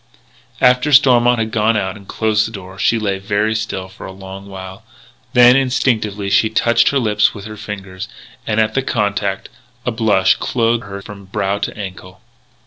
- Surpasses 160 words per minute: Yes, average, 180 wpm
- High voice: No, low, 105 Hz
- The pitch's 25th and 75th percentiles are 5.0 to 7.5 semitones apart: No, average, 2.8 semitones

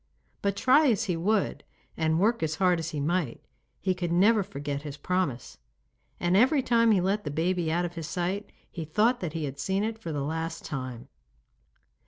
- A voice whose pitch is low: No, medium, 175 Hz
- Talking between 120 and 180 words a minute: No, average, 200 wpm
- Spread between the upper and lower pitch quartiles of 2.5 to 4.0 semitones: No, average, 4.5 semitones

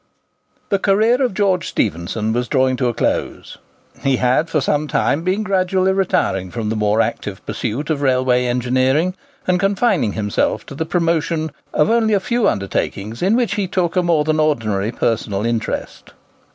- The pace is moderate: Yes, average, 170 wpm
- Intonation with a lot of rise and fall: Yes, wide, 8.1 semitones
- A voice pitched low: No, medium, 150 Hz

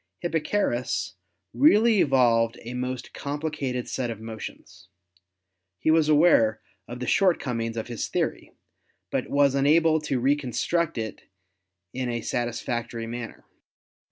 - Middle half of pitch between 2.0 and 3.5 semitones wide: No, average, 4.5 semitones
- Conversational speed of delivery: No, slow, 125 wpm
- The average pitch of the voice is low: Yes, low, 125 Hz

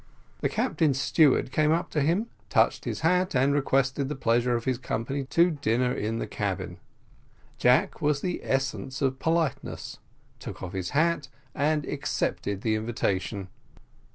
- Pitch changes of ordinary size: Yes, average, 4.4 semitones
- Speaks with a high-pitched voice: No, low, 135 Hz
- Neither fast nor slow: Yes, average, 155 wpm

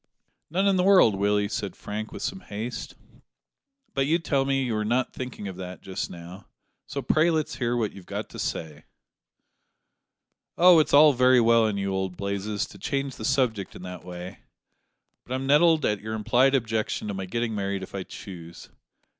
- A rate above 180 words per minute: Yes, average, 190 wpm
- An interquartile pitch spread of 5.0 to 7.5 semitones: Yes, wide, 5.6 semitones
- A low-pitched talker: Yes, low, 110 Hz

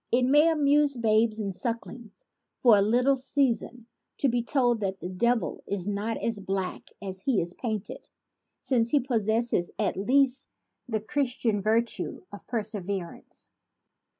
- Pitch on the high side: Yes, high, 230 Hz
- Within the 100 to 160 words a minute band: Yes, average, 150 wpm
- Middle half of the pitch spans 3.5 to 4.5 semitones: Yes, average, 3.8 semitones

